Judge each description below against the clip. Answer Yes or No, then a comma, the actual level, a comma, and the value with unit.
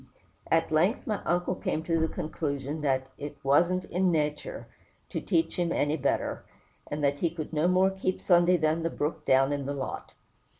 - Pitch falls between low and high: Yes, medium, 160 Hz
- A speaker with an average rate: Yes, average, 185 wpm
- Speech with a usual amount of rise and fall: Yes, average, 3.4 semitones